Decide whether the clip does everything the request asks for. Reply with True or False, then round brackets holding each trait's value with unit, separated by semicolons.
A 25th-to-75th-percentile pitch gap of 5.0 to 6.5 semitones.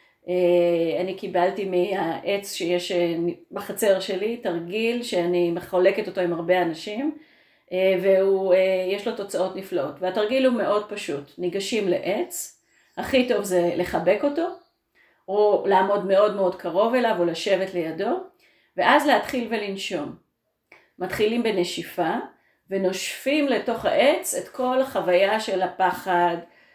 False (3.8 semitones)